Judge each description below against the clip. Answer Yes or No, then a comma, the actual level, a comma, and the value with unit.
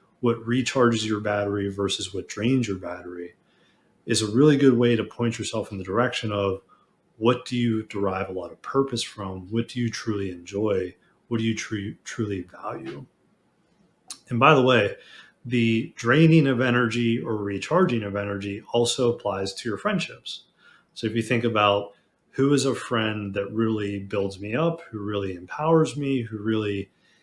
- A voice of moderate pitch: No, low, 115 Hz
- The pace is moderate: Yes, average, 170 wpm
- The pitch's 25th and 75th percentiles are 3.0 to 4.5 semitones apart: Yes, average, 3.5 semitones